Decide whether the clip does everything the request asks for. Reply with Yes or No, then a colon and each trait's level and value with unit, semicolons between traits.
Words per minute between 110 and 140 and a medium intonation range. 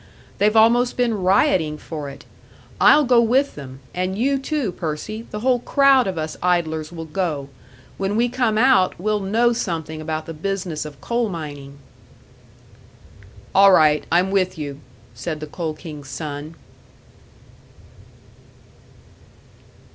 No: slow, 135 wpm; wide, 6.5 semitones